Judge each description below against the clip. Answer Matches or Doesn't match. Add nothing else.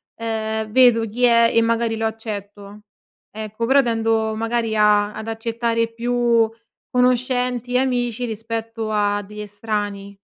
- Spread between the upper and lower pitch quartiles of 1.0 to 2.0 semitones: Matches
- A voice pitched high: Matches